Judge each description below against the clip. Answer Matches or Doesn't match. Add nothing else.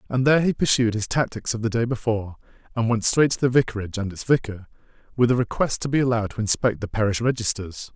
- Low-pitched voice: Matches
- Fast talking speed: Matches